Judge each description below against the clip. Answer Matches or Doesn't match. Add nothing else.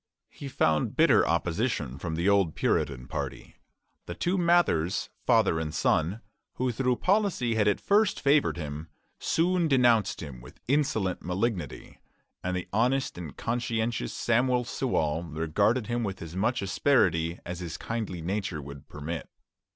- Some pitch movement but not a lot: Doesn't match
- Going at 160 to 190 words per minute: Doesn't match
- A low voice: Matches